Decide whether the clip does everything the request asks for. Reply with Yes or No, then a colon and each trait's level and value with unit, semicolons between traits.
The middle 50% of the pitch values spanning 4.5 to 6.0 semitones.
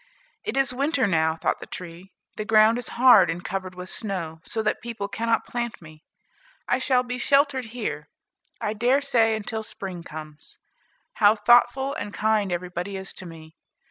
Yes: average, 5.3 semitones